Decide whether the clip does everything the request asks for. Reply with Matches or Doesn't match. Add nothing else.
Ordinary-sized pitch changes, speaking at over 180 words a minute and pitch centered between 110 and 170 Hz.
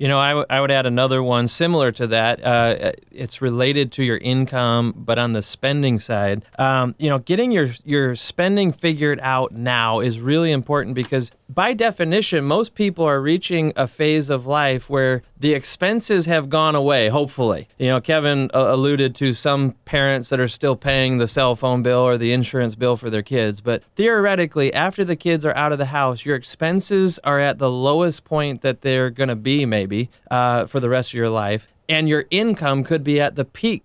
Matches